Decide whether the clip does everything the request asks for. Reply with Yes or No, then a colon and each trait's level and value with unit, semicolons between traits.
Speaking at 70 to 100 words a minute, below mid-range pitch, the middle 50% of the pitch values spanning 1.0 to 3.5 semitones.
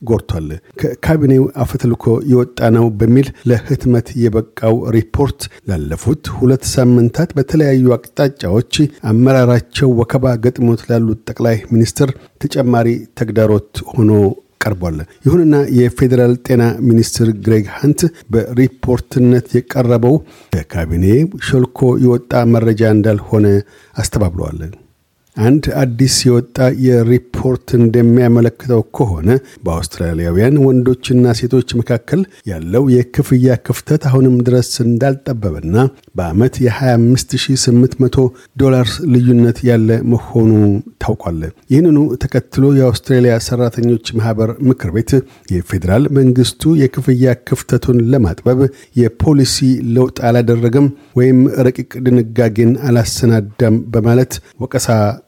Yes: average, 90 wpm; low, 120 Hz; narrow, 2.5 semitones